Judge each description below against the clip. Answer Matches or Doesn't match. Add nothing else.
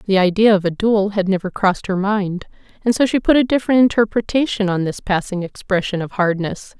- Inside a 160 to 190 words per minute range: Doesn't match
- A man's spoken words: Doesn't match